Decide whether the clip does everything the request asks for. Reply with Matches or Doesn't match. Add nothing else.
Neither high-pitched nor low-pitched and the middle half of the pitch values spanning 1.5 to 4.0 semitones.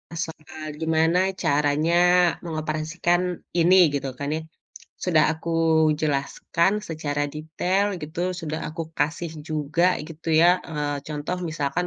Matches